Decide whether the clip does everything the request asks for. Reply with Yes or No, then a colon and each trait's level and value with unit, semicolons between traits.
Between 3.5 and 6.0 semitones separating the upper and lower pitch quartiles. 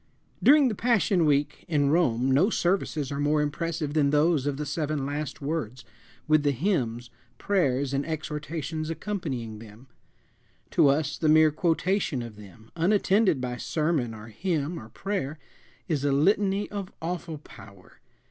Yes: average, 4.1 semitones